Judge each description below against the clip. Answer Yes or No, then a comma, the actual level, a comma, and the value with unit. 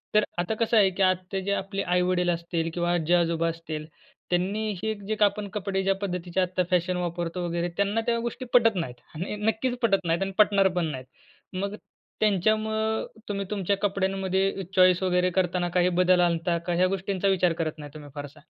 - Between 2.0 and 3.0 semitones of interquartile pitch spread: Yes, narrow, 2.5 semitones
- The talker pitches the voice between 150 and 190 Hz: Yes, medium, 185 Hz